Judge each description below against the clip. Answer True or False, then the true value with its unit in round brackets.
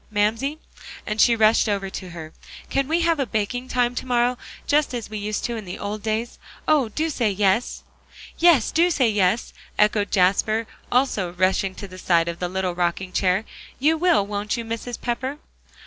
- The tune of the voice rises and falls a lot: False (4.5 semitones)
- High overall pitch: True (215 Hz)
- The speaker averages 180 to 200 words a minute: True (195 wpm)